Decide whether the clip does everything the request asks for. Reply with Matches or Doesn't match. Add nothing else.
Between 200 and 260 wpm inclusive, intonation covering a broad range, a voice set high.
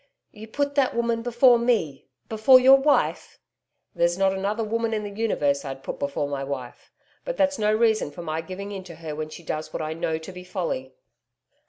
Matches